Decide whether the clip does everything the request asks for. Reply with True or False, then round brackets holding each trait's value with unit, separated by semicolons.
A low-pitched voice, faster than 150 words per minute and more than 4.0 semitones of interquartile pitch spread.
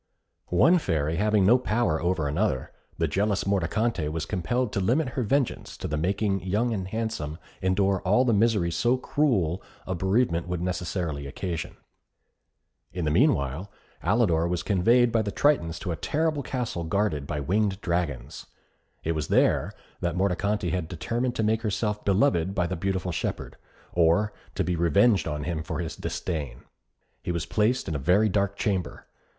True (95 Hz; 165 wpm; 4.5 semitones)